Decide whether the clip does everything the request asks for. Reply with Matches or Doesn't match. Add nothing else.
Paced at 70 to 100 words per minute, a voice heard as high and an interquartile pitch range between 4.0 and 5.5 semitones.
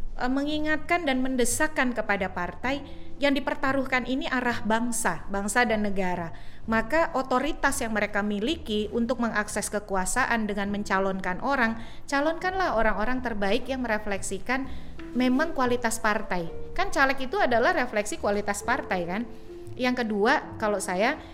Doesn't match